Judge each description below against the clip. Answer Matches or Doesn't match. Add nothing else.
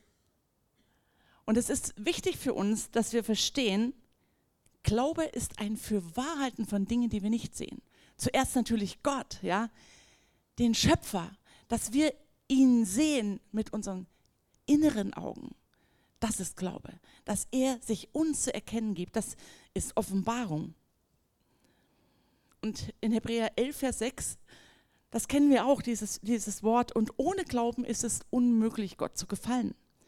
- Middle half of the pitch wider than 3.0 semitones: Matches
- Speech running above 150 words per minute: Doesn't match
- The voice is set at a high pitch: Matches